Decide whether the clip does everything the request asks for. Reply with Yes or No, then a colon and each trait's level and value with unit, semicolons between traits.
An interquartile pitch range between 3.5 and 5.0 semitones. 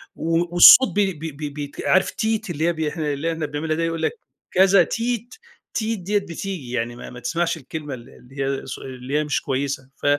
Yes: average, 4.7 semitones